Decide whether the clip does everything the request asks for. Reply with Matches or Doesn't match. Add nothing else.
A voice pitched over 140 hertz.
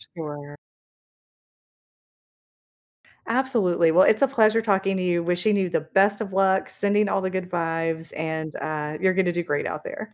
Matches